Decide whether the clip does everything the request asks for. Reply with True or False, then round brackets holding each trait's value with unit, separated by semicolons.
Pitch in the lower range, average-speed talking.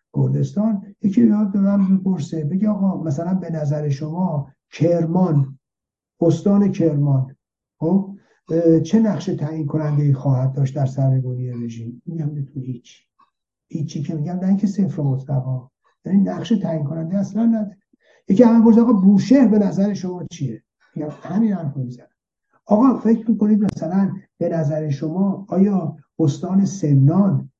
False (170 Hz; 145 wpm)